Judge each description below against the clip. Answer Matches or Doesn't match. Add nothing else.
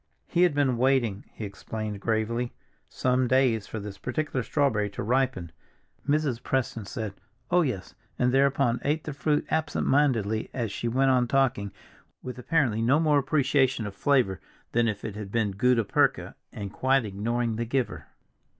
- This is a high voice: Doesn't match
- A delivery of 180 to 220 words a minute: Doesn't match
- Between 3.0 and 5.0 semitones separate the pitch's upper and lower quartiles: Matches